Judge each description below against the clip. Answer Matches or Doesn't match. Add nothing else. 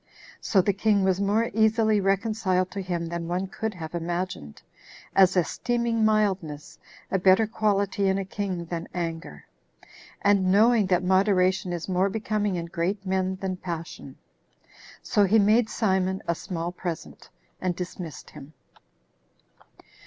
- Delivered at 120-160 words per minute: Matches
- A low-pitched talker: Doesn't match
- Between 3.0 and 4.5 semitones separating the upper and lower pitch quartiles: Doesn't match